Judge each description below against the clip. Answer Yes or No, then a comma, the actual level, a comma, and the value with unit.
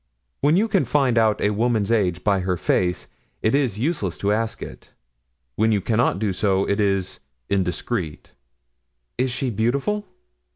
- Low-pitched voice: Yes, low, 110 Hz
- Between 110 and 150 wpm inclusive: No, average, 160 wpm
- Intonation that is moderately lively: Yes, average, 4.1 semitones